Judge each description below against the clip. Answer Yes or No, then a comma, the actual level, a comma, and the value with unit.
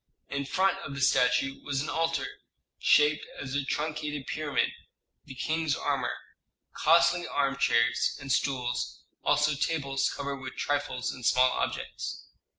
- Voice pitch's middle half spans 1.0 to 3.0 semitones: Yes, narrow, 2.6 semitones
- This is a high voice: No, medium, 140 Hz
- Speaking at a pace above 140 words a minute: No, slow, 135 wpm